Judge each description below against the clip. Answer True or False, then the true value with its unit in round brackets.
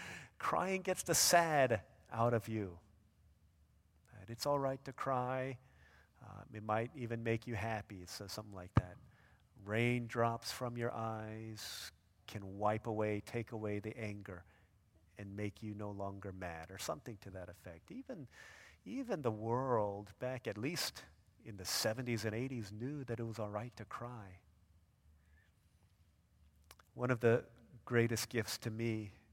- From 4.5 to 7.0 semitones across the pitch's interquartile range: False (4.1 semitones)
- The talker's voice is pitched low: True (110 Hz)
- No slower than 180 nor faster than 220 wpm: False (145 wpm)